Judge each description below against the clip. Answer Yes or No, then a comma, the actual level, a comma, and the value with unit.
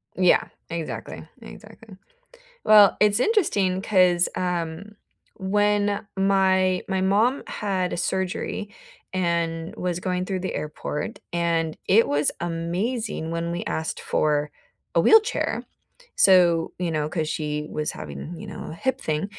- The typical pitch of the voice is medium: Yes, medium, 180 Hz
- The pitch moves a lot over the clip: No, average, 3.3 semitones